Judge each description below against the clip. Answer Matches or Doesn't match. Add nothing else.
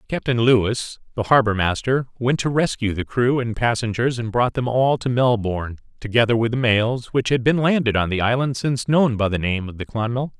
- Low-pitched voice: Matches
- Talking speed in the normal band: Doesn't match